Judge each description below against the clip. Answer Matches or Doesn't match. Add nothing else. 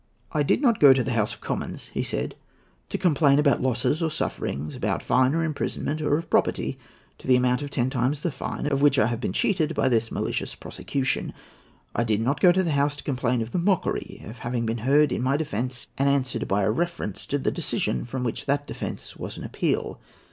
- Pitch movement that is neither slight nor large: Matches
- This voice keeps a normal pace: Doesn't match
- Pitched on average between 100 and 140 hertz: Matches